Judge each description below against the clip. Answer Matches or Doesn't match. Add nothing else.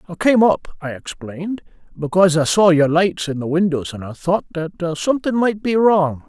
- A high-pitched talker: Doesn't match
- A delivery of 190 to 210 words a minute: Matches